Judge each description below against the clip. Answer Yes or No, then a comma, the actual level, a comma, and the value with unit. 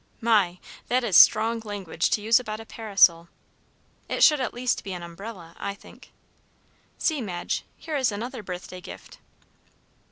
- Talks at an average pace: Yes, average, 155 wpm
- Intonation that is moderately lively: Yes, average, 4.3 semitones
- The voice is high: Yes, high, 215 Hz